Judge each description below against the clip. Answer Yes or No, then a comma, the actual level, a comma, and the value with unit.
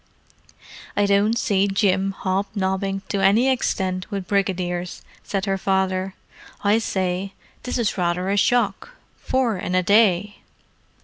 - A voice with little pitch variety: Yes, narrow, 1.5 semitones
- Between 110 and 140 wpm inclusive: Yes, slow, 135 wpm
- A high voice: Yes, high, 195 Hz